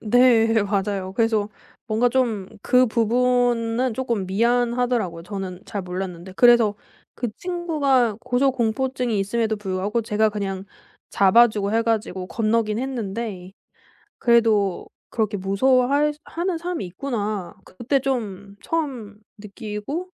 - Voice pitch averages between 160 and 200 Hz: No, high, 225 Hz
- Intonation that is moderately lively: Yes, average, 3.6 semitones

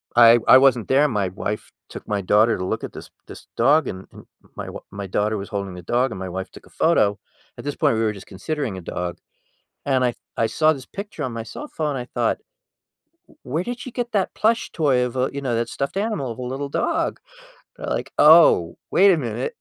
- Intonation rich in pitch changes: Yes, wide, 6.0 semitones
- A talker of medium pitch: No, low, 125 Hz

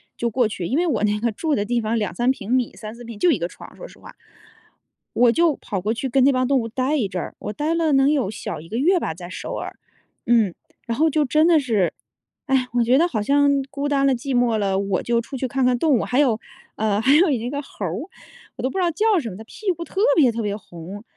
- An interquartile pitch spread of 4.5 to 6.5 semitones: Yes, average, 5.0 semitones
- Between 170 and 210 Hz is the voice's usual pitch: No, high, 245 Hz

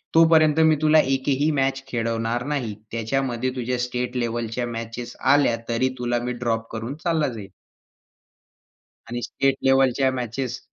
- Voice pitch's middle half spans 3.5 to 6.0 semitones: No, narrow, 2.6 semitones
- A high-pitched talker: No, low, 125 Hz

